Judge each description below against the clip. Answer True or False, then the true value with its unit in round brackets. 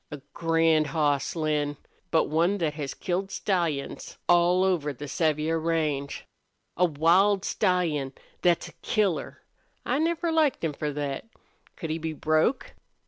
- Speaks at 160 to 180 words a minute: False (140 wpm)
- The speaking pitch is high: False (165 Hz)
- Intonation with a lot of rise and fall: False (3.4 semitones)